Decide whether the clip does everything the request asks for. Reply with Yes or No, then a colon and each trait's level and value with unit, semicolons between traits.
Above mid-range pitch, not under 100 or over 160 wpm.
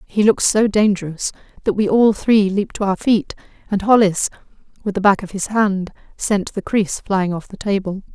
No: high, 200 Hz; average, 200 wpm